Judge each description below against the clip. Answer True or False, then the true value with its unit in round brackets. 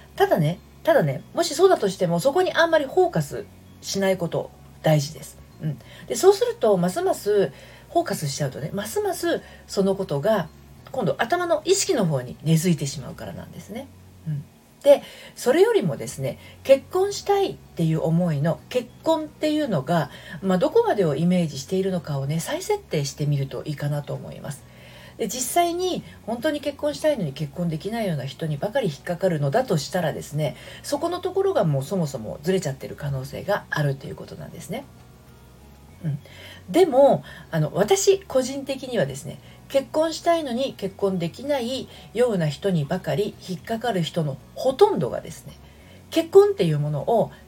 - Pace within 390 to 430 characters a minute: False (375 characters per minute)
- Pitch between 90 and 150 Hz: False (190 Hz)